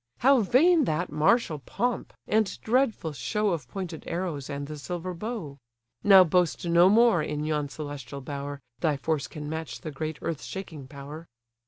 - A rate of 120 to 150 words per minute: No, average, 165 wpm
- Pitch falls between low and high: Yes, medium, 160 Hz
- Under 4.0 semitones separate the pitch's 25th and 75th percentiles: No, average, 4.9 semitones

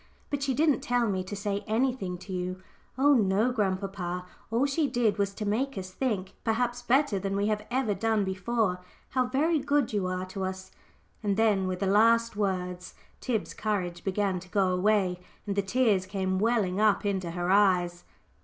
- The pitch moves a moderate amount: Yes, average, 3.9 semitones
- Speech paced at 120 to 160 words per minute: No, average, 185 wpm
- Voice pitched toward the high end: Yes, high, 205 Hz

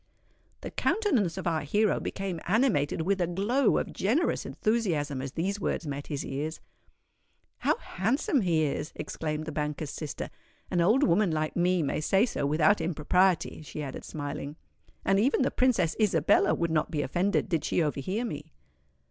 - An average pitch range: Yes, average, 5.0 semitones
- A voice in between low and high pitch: Yes, medium, 170 Hz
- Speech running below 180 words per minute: Yes, average, 165 wpm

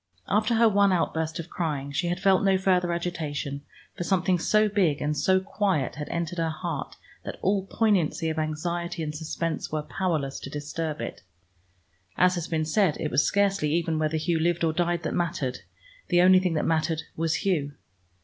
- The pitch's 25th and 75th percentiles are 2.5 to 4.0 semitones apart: Yes, average, 3.1 semitones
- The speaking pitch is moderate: Yes, medium, 170 Hz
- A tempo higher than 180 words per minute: Yes, average, 190 wpm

